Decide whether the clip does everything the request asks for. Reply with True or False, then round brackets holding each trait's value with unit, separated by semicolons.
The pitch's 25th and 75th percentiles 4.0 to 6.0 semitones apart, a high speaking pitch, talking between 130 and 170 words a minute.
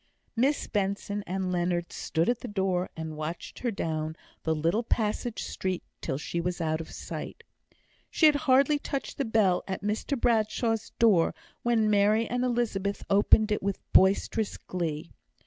True (4.7 semitones; 200 Hz; 160 wpm)